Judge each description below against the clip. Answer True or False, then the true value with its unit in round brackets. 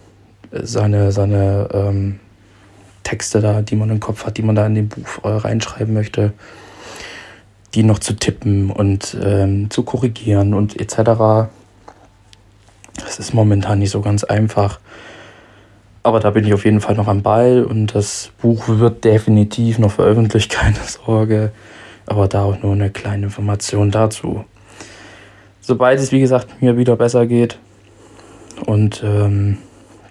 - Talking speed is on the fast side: False (145 wpm)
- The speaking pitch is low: True (105 Hz)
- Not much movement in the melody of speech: True (1.6 semitones)